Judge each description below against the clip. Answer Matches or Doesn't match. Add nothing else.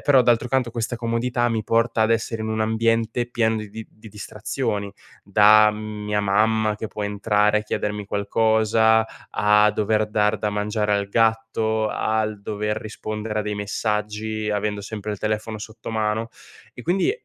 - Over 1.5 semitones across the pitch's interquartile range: Doesn't match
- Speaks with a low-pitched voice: Matches